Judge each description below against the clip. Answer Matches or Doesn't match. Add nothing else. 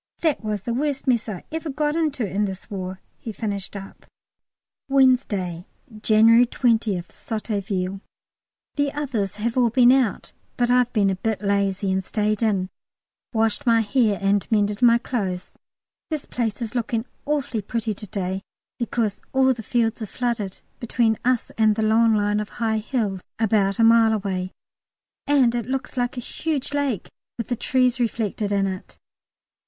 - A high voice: Matches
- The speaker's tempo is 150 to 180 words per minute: Matches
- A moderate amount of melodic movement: Matches